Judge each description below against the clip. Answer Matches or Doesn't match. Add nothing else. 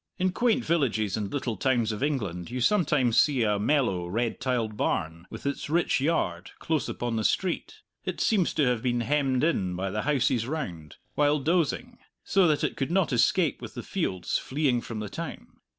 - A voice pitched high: Doesn't match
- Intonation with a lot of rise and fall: Matches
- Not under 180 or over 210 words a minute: Matches